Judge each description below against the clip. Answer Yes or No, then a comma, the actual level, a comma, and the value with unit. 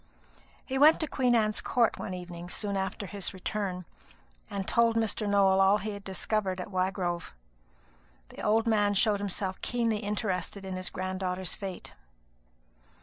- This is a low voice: No, high, 200 Hz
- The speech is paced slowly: No, average, 155 wpm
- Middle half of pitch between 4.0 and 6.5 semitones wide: No, narrow, 2.4 semitones